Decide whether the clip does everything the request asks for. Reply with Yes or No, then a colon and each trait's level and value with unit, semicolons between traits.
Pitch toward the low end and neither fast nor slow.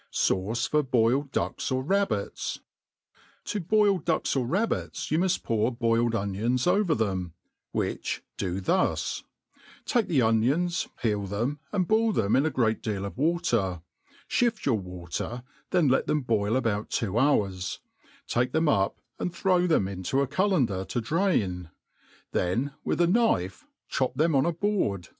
Yes: low, 125 Hz; average, 160 wpm